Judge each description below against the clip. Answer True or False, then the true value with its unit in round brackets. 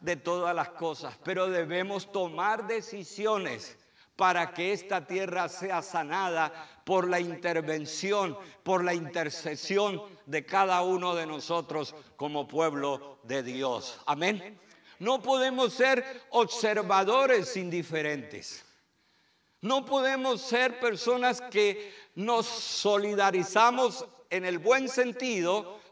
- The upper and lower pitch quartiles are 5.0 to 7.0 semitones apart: True (5.6 semitones)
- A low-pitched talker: False (190 Hz)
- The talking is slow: True (105 wpm)